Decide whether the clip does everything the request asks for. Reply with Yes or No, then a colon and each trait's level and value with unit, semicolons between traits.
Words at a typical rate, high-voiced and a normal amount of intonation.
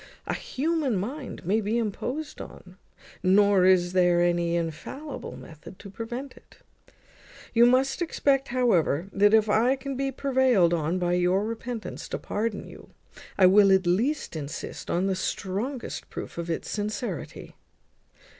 No: average, 145 wpm; high, 205 Hz; wide, 5.9 semitones